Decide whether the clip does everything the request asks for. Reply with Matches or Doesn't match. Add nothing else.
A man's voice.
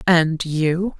Doesn't match